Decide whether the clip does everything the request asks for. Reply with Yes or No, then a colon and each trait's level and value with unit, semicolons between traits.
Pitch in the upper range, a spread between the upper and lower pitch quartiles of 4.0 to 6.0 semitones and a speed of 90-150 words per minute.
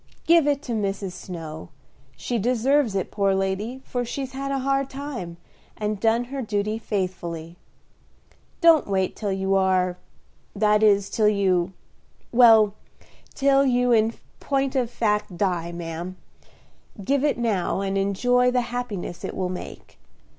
Yes: high, 215 Hz; average, 4.6 semitones; average, 145 wpm